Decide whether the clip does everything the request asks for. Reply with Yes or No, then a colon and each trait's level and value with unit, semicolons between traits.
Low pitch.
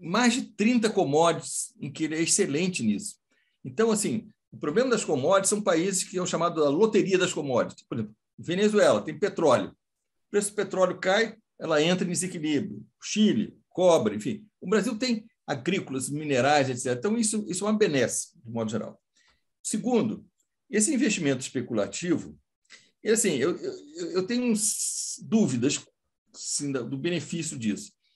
No: high, 190 Hz